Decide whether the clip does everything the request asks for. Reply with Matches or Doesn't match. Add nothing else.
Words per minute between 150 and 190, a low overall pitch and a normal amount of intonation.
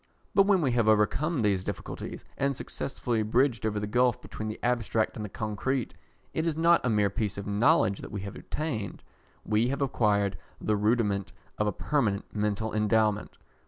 Matches